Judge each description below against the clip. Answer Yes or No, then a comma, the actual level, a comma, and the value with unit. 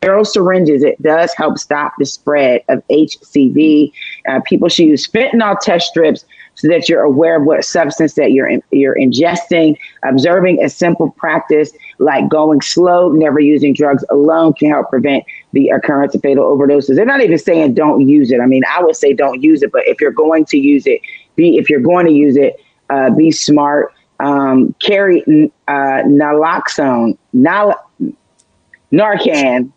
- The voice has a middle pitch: Yes, medium, 165 Hz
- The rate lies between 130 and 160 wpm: No, average, 175 wpm